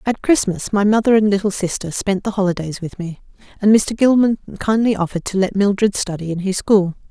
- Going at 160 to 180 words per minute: No, fast, 205 wpm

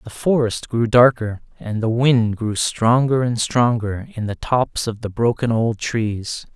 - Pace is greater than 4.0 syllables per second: No, 3.9 syllables/s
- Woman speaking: No, male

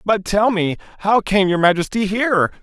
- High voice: Yes, high, 200 Hz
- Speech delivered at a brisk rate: No, average, 185 wpm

